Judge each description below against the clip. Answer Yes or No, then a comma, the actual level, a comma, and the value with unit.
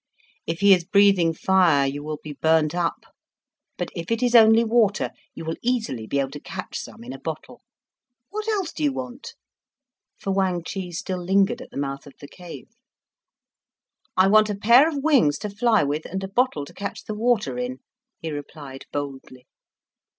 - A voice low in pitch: No, high, 190 Hz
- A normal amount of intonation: No, wide, 7.1 semitones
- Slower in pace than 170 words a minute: No, average, 190 wpm